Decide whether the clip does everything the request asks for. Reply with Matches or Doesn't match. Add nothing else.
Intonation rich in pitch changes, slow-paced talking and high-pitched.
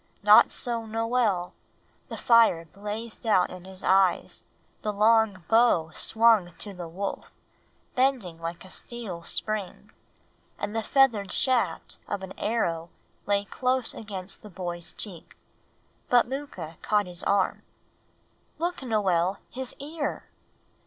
Doesn't match